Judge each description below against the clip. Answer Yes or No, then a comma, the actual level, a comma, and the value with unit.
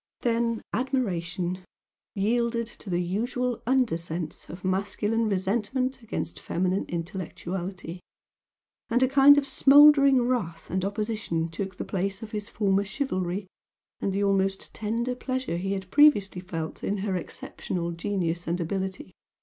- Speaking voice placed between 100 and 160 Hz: No, high, 200 Hz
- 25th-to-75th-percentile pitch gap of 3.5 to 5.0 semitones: Yes, average, 4.7 semitones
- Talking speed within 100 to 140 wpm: Yes, slow, 135 wpm